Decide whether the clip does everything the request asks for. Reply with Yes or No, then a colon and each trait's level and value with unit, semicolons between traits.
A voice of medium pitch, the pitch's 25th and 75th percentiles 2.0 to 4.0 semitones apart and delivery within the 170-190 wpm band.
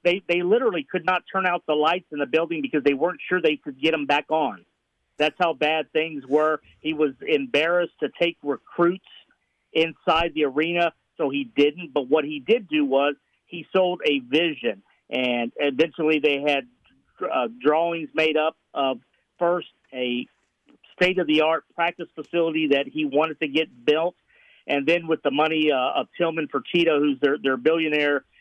Yes: medium, 155 Hz; average, 2.7 semitones; average, 175 wpm